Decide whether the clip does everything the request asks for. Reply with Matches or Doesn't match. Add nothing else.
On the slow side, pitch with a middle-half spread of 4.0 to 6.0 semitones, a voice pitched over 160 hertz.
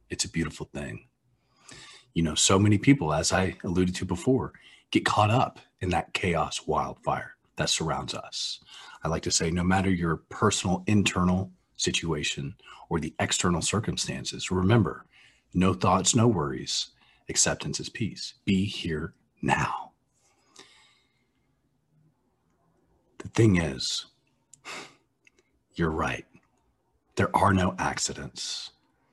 Doesn't match